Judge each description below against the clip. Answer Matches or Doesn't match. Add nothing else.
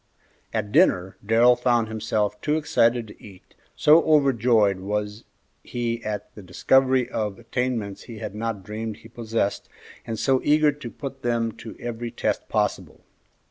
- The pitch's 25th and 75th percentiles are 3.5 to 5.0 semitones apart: Doesn't match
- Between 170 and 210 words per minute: Doesn't match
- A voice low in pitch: Matches